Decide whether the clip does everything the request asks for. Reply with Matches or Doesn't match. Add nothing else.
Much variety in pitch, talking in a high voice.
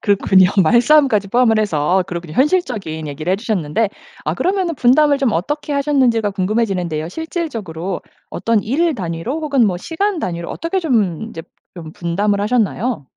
Matches